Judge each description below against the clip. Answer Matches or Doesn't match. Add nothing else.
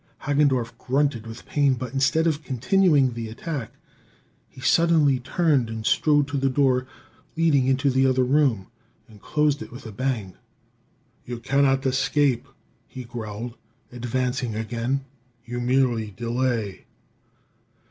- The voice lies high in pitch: Doesn't match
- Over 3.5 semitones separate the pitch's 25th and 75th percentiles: Doesn't match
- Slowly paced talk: Matches